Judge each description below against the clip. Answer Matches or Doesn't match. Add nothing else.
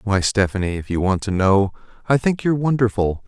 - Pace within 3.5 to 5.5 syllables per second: Doesn't match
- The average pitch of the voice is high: Doesn't match